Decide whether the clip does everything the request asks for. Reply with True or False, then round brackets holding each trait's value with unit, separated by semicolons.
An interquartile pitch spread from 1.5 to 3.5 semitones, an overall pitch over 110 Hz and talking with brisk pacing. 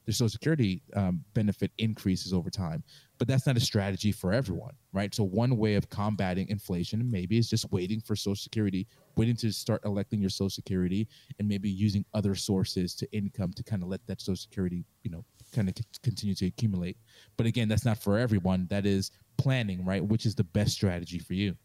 False (3.1 semitones; 105 Hz; 210 wpm)